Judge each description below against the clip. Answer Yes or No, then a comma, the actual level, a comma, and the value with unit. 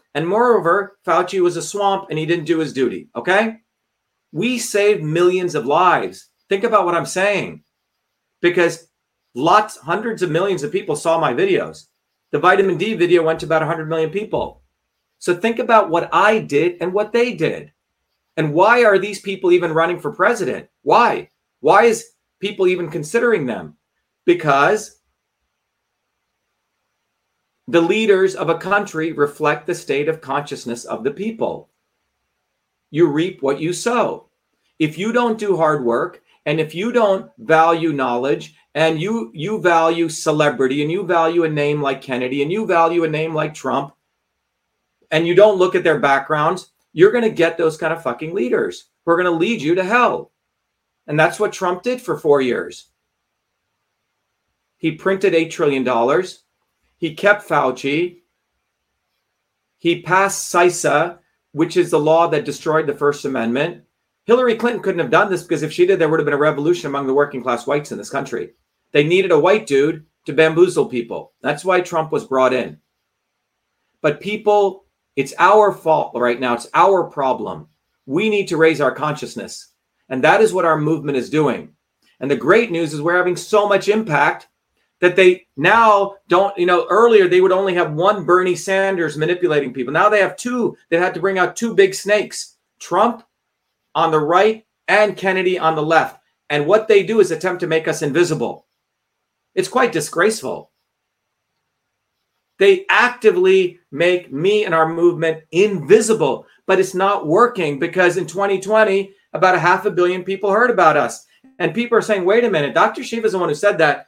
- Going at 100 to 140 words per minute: No, average, 175 wpm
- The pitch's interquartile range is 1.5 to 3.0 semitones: No, average, 4.3 semitones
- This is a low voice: No, medium, 175 Hz